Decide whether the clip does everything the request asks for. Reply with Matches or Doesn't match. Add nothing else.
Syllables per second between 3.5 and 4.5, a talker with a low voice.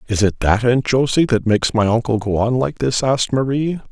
Doesn't match